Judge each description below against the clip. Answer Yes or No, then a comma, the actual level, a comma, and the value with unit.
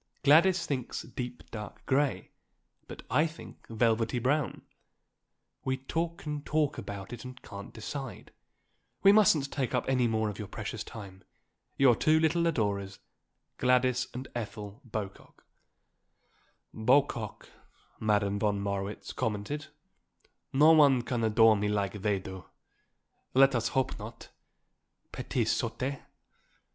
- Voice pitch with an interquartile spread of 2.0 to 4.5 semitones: No, average, 5.1 semitones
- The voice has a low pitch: Yes, low, 120 Hz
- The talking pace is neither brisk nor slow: No, slow, 125 wpm